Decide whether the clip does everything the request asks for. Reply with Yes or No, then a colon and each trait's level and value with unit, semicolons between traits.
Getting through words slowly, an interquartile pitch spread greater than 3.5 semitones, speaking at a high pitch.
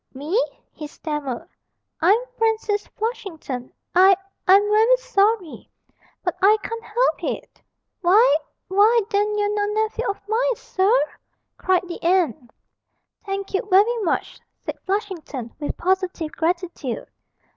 Yes: slow, 125 wpm; average, 4.0 semitones; very high, 395 Hz